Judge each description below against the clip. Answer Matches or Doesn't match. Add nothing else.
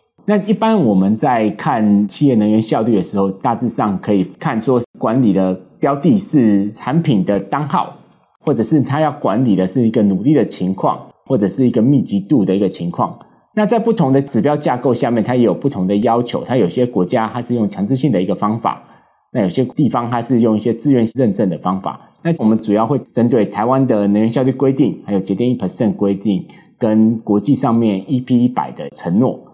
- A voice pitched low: Matches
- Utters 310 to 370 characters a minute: Matches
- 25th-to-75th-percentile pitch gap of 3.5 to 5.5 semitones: Matches